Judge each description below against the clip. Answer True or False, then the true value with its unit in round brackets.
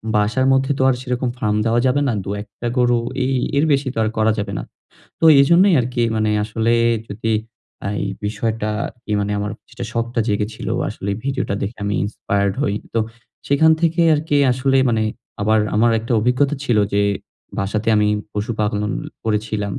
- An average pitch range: True (3.6 semitones)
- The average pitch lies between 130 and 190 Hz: False (115 Hz)